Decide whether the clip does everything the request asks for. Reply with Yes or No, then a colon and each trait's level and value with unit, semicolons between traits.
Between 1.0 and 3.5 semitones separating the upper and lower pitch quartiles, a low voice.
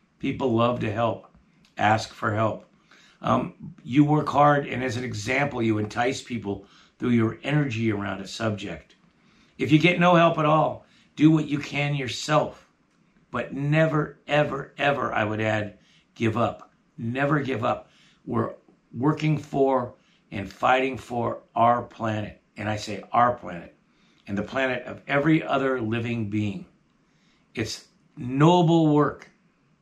No: average, 4.9 semitones; low, 130 Hz